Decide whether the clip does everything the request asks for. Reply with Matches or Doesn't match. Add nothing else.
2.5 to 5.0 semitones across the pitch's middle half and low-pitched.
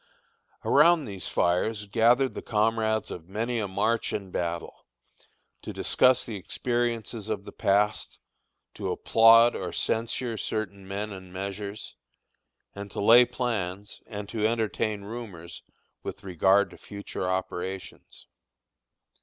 Matches